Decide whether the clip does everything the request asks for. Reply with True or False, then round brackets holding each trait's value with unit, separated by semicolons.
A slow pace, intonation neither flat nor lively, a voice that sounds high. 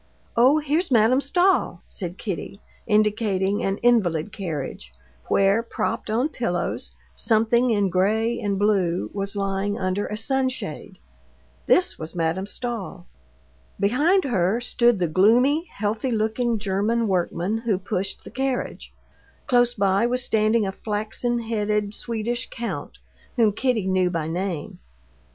True (130 wpm; 3.8 semitones; 215 Hz)